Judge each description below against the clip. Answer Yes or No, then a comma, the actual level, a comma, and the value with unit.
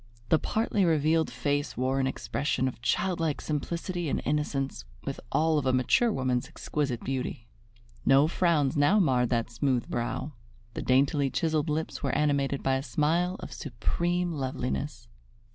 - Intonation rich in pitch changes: No, average, 3.6 semitones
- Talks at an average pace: Yes, average, 150 wpm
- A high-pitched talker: No, medium, 145 Hz